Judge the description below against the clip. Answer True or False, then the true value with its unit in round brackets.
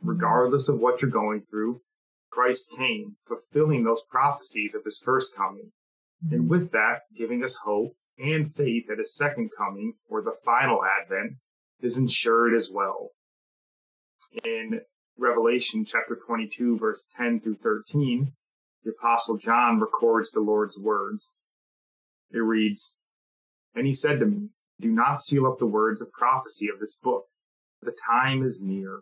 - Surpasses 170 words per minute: False (150 wpm)